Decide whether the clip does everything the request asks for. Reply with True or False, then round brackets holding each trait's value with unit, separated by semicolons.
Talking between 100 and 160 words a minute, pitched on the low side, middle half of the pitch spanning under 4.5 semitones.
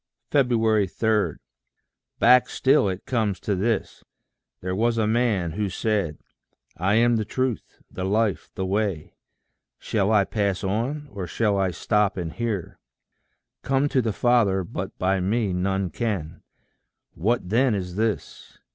True (140 wpm; 105 Hz; 3.6 semitones)